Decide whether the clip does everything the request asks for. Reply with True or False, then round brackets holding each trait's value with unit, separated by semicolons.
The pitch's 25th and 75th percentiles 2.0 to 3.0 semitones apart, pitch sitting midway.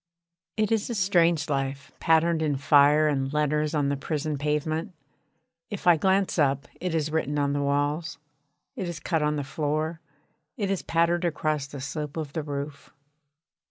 True (2.7 semitones; 150 Hz)